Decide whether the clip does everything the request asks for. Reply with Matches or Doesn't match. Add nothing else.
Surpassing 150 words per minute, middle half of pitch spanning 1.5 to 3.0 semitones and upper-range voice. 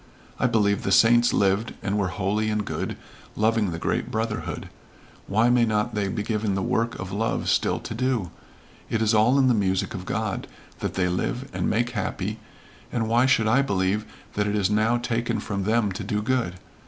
Doesn't match